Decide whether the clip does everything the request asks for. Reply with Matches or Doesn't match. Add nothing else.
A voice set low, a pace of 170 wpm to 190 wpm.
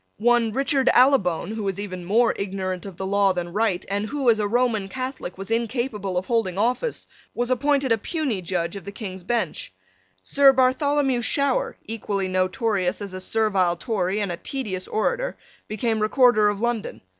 Doesn't match